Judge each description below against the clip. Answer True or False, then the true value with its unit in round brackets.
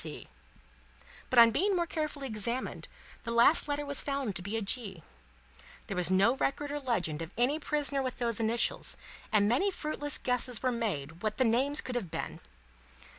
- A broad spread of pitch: False (5.0 semitones)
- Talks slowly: False (175 wpm)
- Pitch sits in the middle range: False (245 Hz)